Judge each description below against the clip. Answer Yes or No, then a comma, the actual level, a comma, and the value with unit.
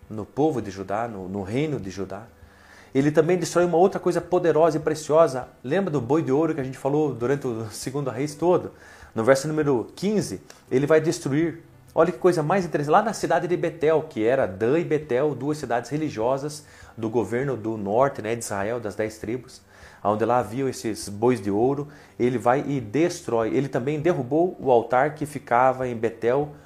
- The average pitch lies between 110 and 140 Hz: Yes, low, 135 Hz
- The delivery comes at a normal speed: No, fast, 195 wpm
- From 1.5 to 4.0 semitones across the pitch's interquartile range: No, average, 5.2 semitones